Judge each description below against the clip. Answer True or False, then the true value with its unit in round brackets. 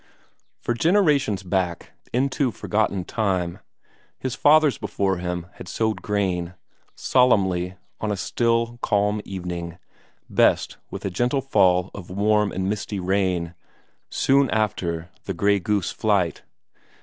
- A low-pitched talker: True (100 Hz)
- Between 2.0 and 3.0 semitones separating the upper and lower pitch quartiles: False (4.3 semitones)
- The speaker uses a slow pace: True (125 wpm)